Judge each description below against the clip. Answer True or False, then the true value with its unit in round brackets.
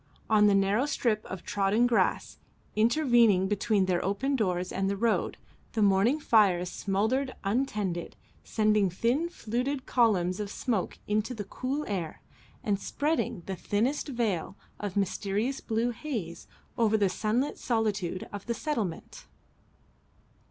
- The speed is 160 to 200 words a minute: False (135 wpm)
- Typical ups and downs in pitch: True (3.7 semitones)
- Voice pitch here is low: False (215 Hz)